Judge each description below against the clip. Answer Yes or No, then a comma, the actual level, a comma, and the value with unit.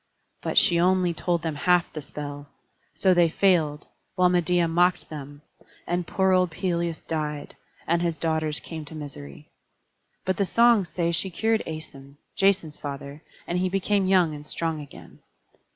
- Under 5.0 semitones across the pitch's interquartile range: Yes, average, 3.2 semitones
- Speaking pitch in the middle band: Yes, medium, 170 Hz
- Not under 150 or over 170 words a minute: Yes, average, 160 wpm